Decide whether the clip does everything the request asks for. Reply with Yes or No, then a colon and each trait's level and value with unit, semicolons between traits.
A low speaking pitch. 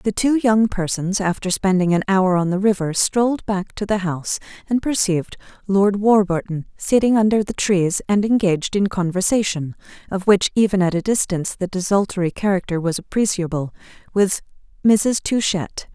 No: high, 195 Hz